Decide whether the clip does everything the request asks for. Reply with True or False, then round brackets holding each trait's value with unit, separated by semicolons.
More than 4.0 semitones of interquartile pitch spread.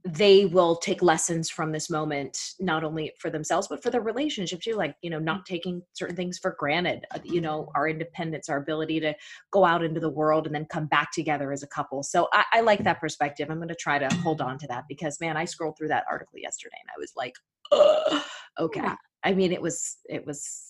False (3.4 semitones)